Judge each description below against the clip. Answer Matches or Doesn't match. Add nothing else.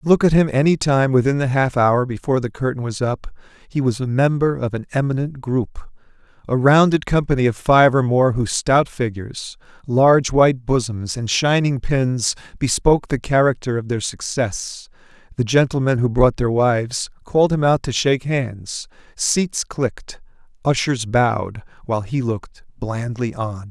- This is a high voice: Doesn't match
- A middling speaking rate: Matches